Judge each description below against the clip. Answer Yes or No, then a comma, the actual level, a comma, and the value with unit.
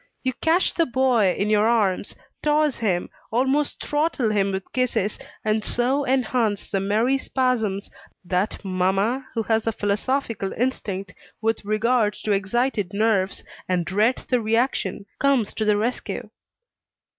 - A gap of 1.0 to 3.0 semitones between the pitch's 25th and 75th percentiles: No, average, 4.1 semitones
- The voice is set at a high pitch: Yes, high, 220 Hz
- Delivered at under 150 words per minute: Yes, average, 140 wpm